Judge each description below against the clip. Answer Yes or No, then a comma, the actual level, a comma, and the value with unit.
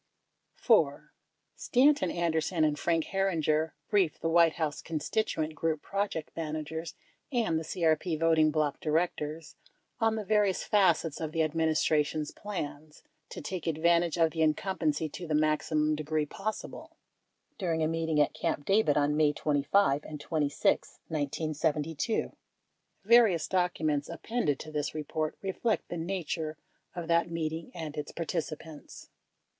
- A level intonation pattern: Yes, narrow, 2.2 semitones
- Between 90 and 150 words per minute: Yes, slow, 135 wpm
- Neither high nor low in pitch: Yes, medium, 160 Hz